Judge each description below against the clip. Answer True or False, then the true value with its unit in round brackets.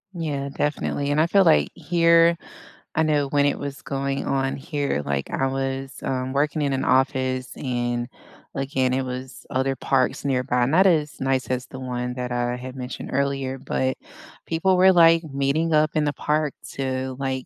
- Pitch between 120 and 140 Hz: True (135 Hz)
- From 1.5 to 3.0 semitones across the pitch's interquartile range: True (2.5 semitones)